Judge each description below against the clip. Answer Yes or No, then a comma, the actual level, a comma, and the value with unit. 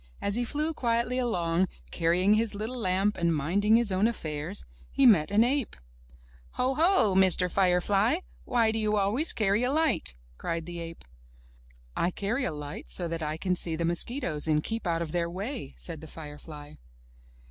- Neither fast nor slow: Yes, average, 180 wpm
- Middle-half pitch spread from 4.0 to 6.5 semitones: Yes, wide, 5.6 semitones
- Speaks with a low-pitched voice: No, high, 190 Hz